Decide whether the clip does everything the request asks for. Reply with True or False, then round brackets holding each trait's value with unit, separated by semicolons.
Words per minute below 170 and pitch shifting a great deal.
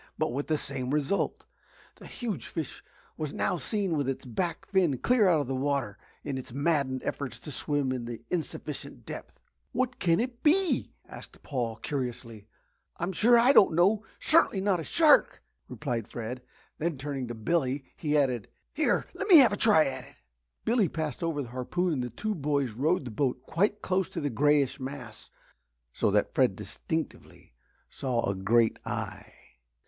False (175 wpm; 6.3 semitones)